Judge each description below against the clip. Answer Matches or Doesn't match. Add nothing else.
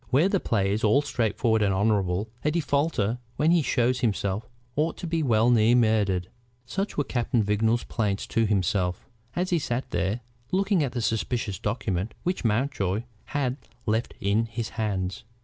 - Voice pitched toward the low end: Matches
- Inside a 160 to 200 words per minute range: Matches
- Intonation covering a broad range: Doesn't match